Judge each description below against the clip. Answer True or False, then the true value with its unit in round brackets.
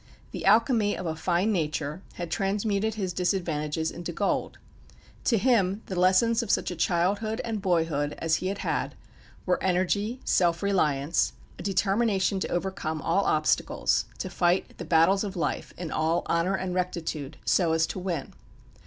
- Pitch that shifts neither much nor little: True (3.4 semitones)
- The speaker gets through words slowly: False (160 wpm)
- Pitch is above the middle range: False (180 Hz)